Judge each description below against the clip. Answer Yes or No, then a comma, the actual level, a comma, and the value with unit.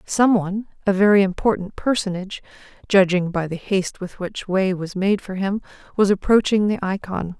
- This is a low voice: No, high, 195 Hz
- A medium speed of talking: Yes, average, 160 wpm